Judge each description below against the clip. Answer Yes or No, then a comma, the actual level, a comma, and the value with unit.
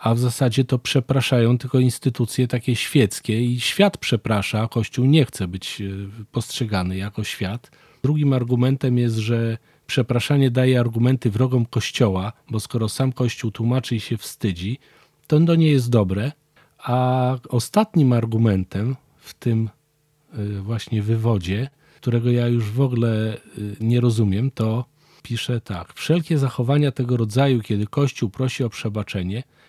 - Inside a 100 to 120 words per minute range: No, average, 135 wpm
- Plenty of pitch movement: No, average, 3.2 semitones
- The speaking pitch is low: Yes, low, 120 Hz